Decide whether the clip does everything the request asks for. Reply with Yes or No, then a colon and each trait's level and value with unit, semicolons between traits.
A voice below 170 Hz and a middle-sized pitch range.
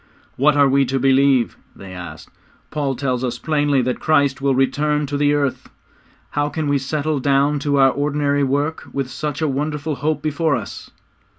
No: medium, 140 Hz; narrow, 1.8 semitones